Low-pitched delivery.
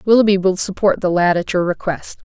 No: high, 190 Hz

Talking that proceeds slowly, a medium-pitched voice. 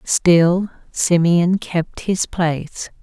Yes: slow, 100 wpm; medium, 175 Hz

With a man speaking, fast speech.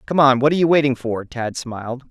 Yes: male; fast, 255 wpm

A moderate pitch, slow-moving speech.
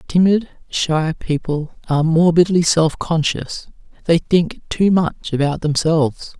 Yes: medium, 165 Hz; slow, 120 wpm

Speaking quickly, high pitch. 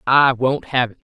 No: fast, 215 wpm; low, 130 Hz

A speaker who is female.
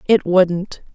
Yes: female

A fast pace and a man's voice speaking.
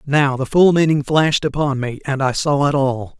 Yes: fast, 225 wpm; male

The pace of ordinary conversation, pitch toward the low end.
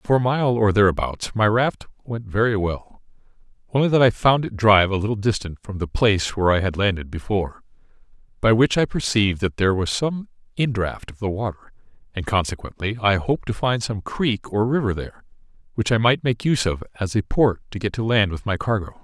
No: fast, 210 wpm; low, 105 Hz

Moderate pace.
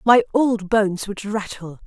Yes: average, 160 wpm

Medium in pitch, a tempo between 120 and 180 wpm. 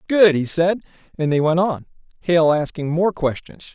Yes: medium, 170 Hz; average, 160 wpm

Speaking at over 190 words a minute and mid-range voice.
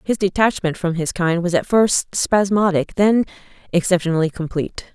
No: average, 145 wpm; medium, 180 Hz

